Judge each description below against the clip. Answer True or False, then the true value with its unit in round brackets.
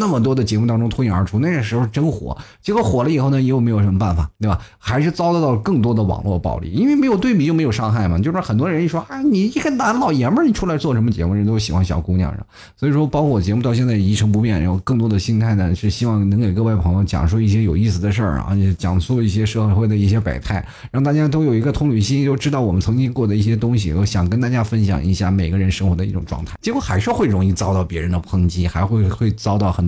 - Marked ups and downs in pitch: False (5.0 semitones)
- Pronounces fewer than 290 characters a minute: False (415 characters per minute)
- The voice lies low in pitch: True (110 Hz)